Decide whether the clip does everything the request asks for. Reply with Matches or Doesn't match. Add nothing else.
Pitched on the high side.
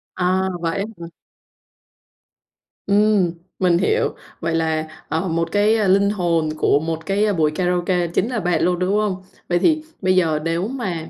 Doesn't match